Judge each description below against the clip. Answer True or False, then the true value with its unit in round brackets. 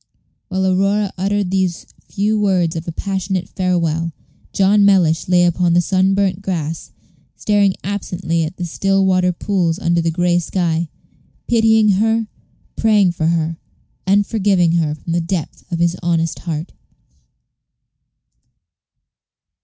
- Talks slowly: True (130 wpm)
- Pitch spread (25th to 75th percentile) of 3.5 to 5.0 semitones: False (2.8 semitones)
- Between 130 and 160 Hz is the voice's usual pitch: False (180 Hz)